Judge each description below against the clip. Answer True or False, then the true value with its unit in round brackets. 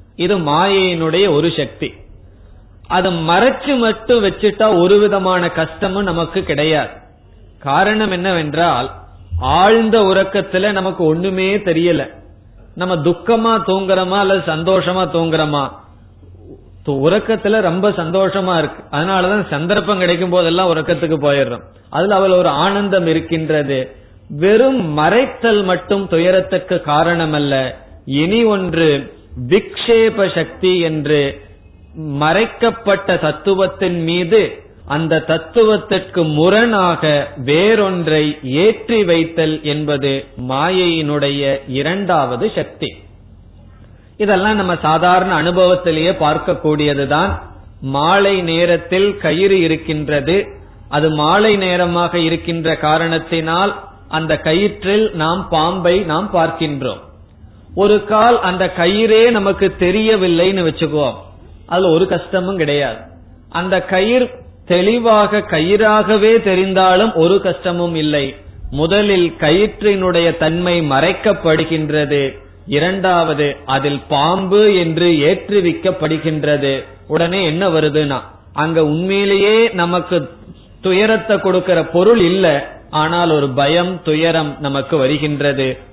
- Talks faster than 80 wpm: True (90 wpm)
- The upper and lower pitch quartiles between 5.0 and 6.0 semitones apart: False (4.4 semitones)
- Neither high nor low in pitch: True (170 Hz)